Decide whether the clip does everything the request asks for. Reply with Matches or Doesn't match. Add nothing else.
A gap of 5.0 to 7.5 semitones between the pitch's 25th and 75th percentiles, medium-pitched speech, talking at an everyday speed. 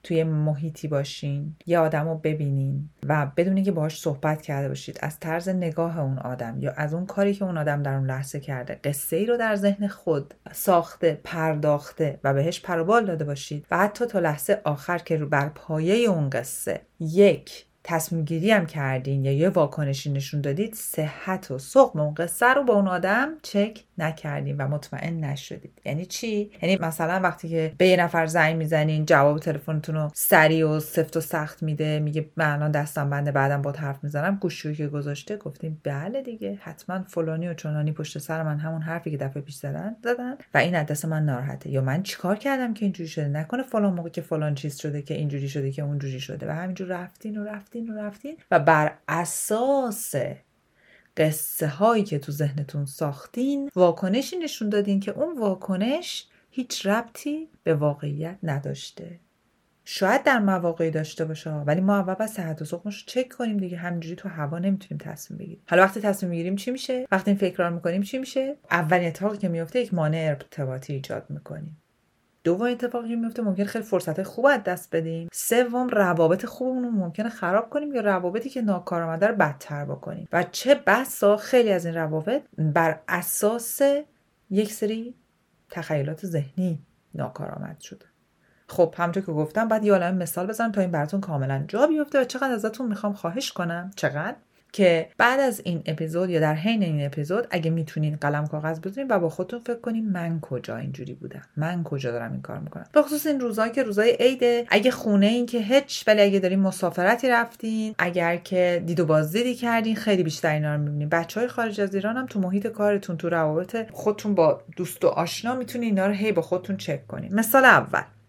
Doesn't match